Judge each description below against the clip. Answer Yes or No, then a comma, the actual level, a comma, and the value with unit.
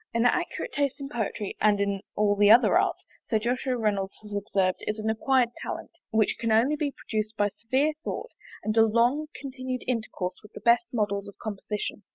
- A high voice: Yes, high, 225 Hz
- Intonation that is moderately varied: Yes, average, 3.5 semitones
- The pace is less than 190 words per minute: No, average, 195 wpm